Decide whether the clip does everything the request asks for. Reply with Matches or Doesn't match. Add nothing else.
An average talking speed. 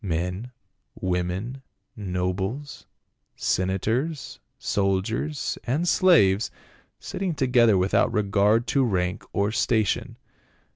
Doesn't match